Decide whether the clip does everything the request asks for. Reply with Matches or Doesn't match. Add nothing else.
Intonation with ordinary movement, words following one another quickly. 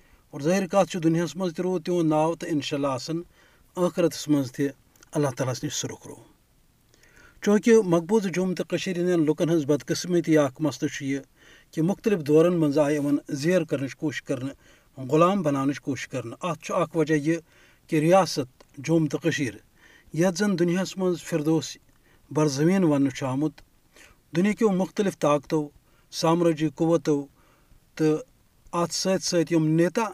Doesn't match